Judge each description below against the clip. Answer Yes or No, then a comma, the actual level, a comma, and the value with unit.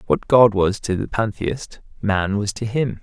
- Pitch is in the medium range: No, low, 105 Hz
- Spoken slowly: No, average, 200 wpm